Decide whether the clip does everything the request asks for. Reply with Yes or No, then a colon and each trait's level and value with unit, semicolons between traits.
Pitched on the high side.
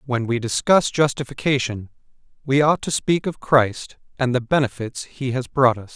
No: low, 130 Hz